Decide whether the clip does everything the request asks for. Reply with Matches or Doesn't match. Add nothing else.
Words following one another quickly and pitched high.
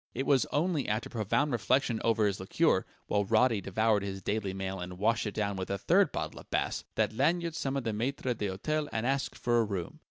Doesn't match